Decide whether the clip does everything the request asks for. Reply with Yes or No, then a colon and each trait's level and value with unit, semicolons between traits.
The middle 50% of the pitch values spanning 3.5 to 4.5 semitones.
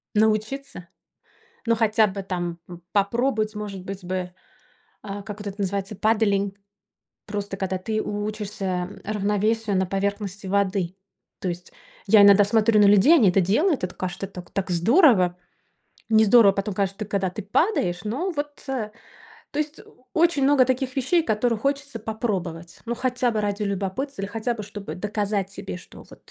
No: average, 2.8 semitones